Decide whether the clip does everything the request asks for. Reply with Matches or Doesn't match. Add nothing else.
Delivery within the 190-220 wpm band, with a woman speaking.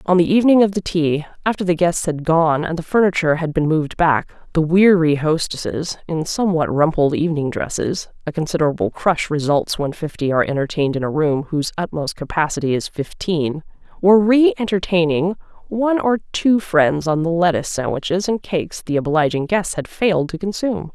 Doesn't match